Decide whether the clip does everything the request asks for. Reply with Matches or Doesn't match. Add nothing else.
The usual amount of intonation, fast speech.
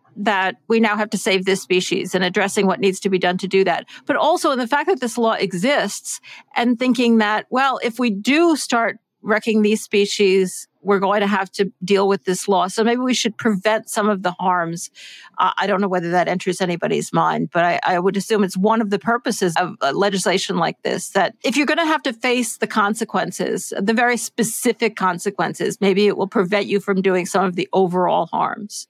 Matches